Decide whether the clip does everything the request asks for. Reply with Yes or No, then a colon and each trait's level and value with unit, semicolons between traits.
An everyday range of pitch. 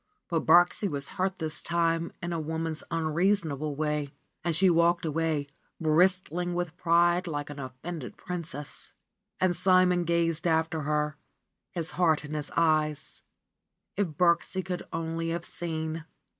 No: narrow, 2.3 semitones